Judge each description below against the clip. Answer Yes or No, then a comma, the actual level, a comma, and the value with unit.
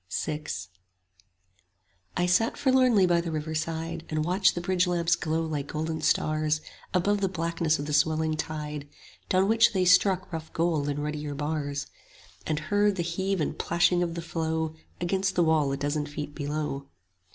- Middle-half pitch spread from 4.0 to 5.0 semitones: No, average, 2.8 semitones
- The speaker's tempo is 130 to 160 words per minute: No, average, 175 wpm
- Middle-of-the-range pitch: Yes, medium, 160 Hz